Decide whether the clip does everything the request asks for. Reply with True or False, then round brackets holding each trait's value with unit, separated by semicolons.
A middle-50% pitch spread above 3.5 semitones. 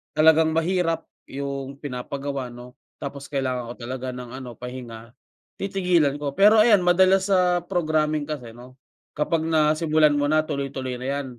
True (4.0 semitones)